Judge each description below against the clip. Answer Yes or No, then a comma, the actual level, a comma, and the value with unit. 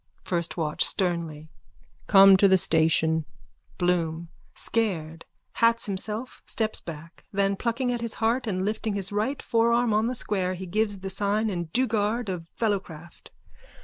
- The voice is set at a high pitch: Yes, high, 195 Hz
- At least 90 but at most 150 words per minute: Yes, average, 145 wpm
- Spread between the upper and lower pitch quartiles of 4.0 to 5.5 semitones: Yes, average, 4.5 semitones